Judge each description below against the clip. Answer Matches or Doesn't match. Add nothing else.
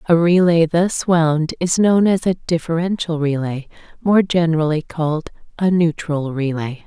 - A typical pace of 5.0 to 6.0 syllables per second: Doesn't match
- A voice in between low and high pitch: Matches